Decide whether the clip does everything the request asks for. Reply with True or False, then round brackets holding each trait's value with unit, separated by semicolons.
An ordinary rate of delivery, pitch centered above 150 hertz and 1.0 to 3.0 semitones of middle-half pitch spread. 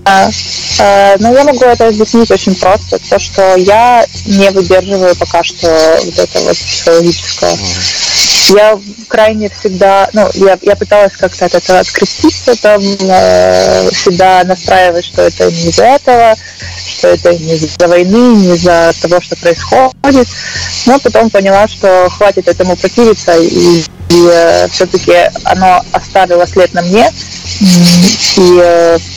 False (135 wpm; 185 Hz; 3.5 semitones)